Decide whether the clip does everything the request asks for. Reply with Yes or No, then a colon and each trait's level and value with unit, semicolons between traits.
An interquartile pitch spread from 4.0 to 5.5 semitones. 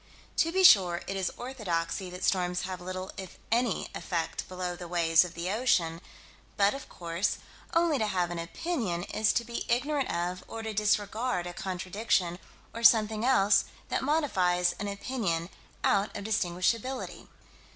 Yes: average, 4.6 semitones